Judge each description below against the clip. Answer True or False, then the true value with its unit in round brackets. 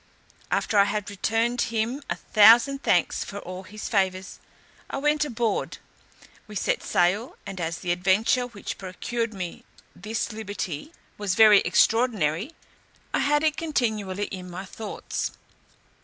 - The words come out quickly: False (140 wpm)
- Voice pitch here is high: True (210 Hz)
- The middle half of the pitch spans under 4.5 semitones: True (4.0 semitones)